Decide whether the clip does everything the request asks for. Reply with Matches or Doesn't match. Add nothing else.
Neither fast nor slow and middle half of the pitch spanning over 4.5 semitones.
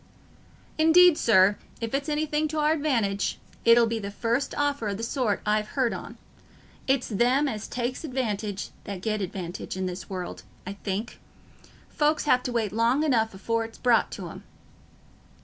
Matches